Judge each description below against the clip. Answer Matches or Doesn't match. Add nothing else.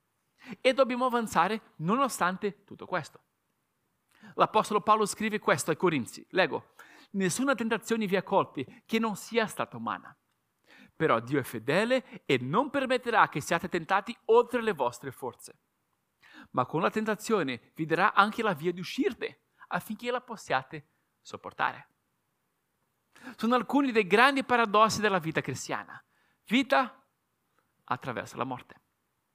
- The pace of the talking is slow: Doesn't match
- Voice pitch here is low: Doesn't match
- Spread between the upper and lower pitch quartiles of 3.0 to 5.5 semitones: Matches